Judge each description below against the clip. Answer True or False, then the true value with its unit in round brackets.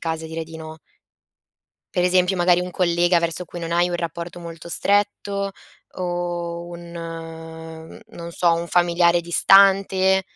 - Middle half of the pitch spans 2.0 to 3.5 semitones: False (1.3 semitones)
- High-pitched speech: False (170 Hz)